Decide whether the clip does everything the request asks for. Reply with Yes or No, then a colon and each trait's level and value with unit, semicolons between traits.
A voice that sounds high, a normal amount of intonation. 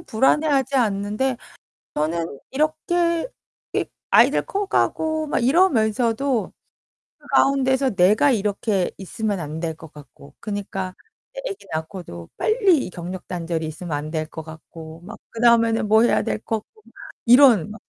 No: high, 215 Hz; wide, 7.9 semitones